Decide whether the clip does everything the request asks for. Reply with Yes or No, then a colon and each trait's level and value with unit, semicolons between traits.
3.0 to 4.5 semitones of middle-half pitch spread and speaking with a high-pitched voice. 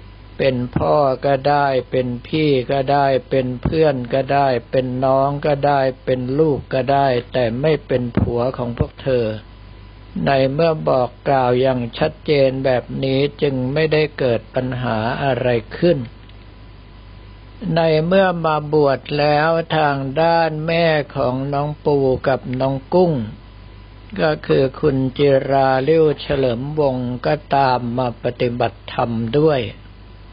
No: average, 3.3 semitones; low, 135 Hz